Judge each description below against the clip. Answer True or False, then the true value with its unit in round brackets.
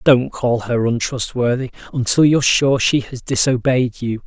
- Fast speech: False (155 wpm)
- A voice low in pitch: True (125 Hz)